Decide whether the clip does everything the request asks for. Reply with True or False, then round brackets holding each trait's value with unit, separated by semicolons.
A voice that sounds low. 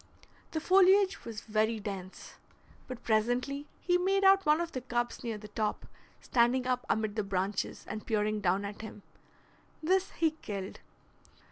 False (235 Hz)